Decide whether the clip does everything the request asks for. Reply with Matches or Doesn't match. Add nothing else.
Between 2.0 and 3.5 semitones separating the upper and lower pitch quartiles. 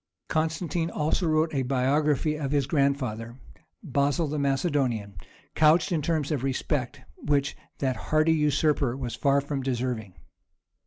Matches